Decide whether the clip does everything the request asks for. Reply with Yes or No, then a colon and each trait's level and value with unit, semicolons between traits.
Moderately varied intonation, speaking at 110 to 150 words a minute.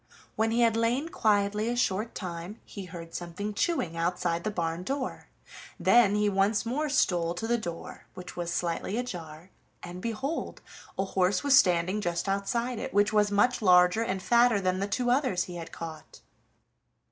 No: average, 4.5 semitones; average, 175 wpm